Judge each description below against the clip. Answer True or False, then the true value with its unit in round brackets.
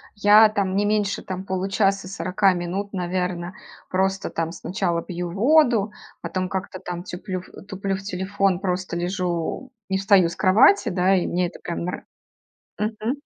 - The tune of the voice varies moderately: False (2.0 semitones)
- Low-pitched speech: False (190 Hz)